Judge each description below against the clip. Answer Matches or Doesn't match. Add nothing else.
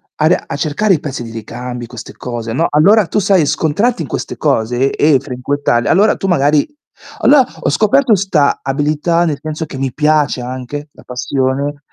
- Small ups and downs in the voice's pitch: Doesn't match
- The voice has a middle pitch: Matches